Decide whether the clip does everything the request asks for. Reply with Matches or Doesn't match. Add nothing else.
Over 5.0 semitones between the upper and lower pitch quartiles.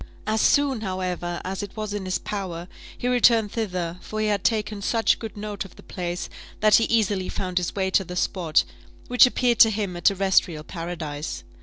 Doesn't match